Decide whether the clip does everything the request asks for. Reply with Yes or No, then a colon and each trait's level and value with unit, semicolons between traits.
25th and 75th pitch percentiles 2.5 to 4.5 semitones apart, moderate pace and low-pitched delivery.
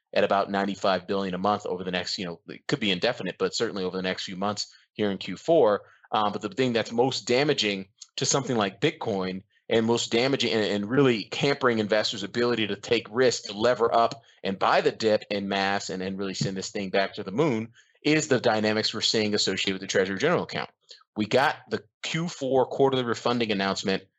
No: average, 3.5 semitones; fast, 210 wpm; low, 110 Hz